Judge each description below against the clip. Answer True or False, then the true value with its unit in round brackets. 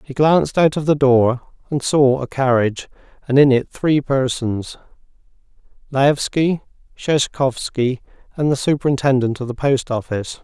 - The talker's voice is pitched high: False (135 Hz)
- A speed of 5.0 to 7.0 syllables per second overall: False (4.7 syllables/s)